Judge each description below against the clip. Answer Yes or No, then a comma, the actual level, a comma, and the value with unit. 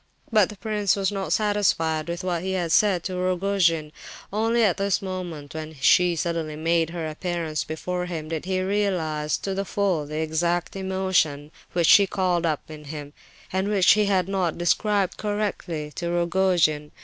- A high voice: No, medium, 180 Hz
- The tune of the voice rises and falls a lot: No, average, 3.4 semitones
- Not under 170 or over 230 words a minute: Yes, average, 175 wpm